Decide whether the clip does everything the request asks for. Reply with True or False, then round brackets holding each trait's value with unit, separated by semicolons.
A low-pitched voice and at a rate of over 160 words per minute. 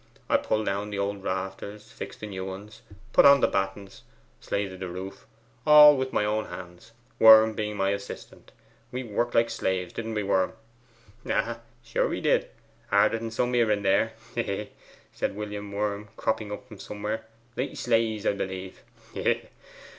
True (105 Hz; 175 wpm)